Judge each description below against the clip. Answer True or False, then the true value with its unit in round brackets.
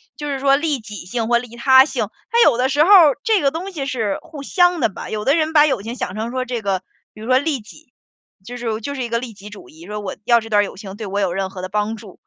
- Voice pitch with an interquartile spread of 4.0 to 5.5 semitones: True (5.2 semitones)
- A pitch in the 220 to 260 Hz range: True (240 Hz)